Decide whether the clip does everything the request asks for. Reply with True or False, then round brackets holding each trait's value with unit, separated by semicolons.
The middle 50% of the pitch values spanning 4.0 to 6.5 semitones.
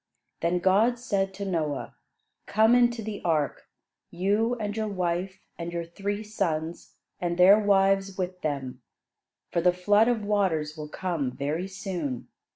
False (3.4 semitones)